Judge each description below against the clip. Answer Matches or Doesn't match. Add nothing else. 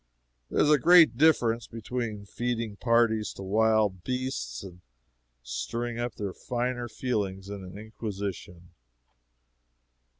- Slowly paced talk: Matches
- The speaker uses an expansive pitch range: Doesn't match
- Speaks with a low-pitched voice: Matches